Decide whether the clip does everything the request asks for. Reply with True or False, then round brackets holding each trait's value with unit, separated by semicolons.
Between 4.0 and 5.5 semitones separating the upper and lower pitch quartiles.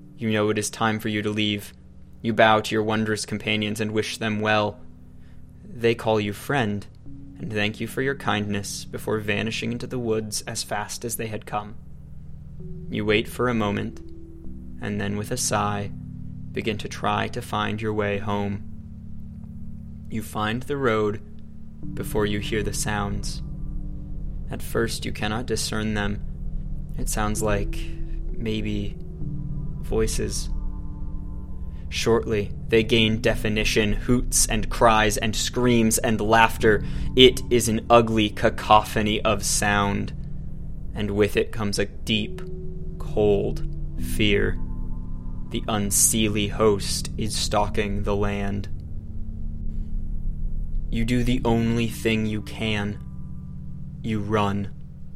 True (4.9 semitones)